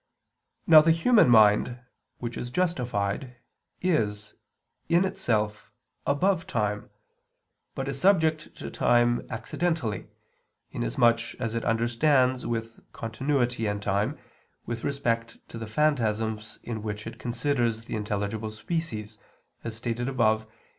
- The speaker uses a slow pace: Yes, slow, 125 wpm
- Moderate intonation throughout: Yes, average, 4.2 semitones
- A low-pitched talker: Yes, low, 115 Hz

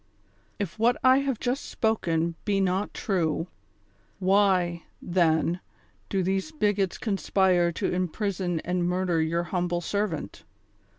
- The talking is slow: Yes, slow, 120 wpm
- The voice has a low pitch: No, medium, 185 Hz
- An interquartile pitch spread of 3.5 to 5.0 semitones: No, average, 2.9 semitones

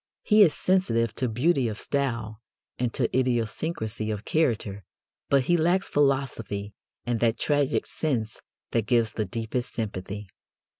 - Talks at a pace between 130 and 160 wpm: Yes, average, 140 wpm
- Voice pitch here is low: Yes, low, 120 Hz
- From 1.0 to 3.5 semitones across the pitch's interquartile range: No, average, 4.6 semitones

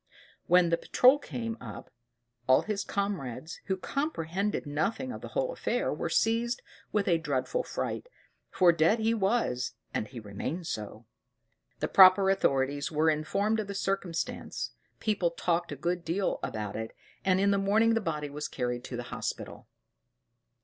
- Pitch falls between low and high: Yes, medium, 180 Hz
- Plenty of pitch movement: Yes, wide, 6.0 semitones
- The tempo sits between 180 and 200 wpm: No, average, 160 wpm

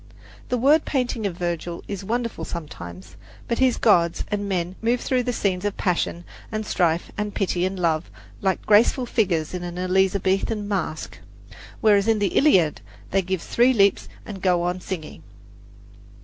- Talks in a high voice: Yes, high, 195 Hz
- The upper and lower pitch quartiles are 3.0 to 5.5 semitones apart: Yes, average, 3.8 semitones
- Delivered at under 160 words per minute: No, average, 165 wpm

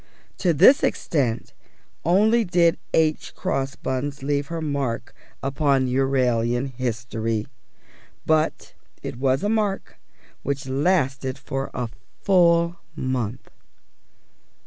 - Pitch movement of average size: Yes, average, 4.5 semitones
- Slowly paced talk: Yes, slow, 100 wpm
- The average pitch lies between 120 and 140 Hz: Yes, low, 135 Hz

